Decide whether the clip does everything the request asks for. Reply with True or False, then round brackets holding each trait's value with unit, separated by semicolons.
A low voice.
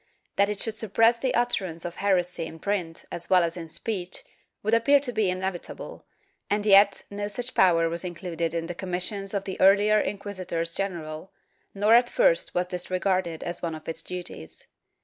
False (190 Hz)